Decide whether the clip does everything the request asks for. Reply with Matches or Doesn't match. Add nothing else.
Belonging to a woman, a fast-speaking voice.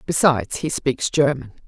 Doesn't match